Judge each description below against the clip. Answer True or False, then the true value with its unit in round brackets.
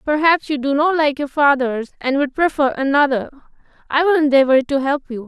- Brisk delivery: False (195 wpm)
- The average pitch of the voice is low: False (280 Hz)